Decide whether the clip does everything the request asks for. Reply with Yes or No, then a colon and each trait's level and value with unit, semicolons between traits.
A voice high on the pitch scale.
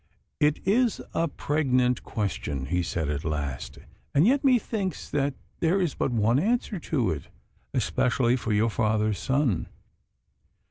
No: low, 125 Hz